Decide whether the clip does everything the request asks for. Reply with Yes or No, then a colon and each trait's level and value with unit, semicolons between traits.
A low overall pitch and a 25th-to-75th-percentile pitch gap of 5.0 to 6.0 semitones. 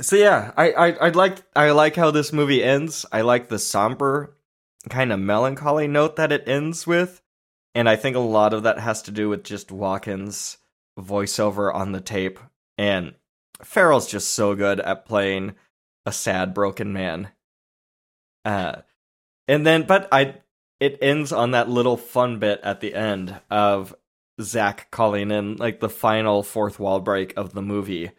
Yes: low, 110 Hz; wide, 5.5 semitones